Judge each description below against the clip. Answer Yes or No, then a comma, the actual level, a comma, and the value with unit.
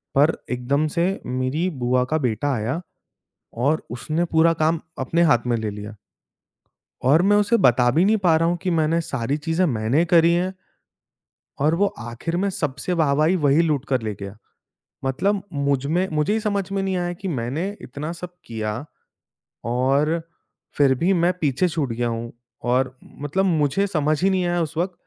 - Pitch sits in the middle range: Yes, medium, 155 Hz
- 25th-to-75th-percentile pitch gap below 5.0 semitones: No, average, 5.3 semitones